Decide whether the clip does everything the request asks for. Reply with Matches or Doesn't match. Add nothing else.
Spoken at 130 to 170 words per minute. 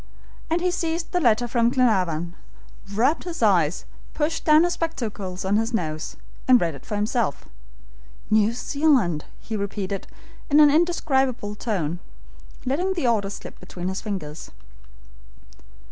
Matches